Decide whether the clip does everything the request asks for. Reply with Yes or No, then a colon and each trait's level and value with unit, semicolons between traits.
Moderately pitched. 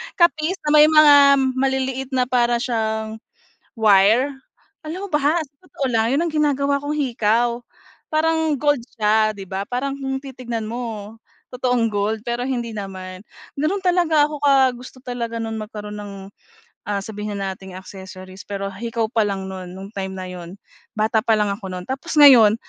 No: high, 235 Hz